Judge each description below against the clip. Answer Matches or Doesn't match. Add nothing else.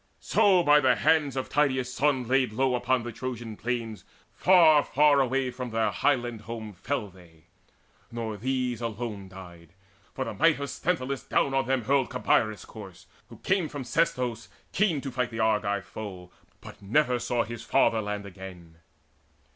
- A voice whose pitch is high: Doesn't match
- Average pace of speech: Matches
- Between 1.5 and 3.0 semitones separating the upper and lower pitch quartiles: Doesn't match